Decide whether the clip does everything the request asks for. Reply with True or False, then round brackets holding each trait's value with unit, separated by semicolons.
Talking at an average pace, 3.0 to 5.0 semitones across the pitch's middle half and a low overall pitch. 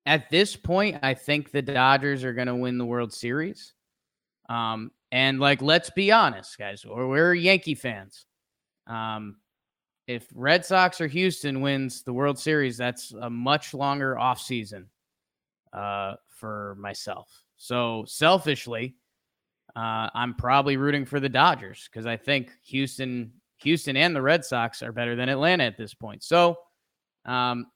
True (155 wpm; 3.7 semitones; 130 Hz)